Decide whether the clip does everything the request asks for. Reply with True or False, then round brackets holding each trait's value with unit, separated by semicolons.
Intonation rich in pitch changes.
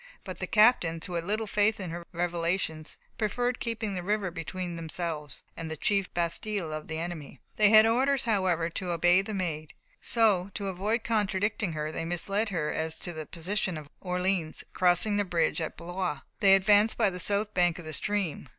False (3.8 semitones)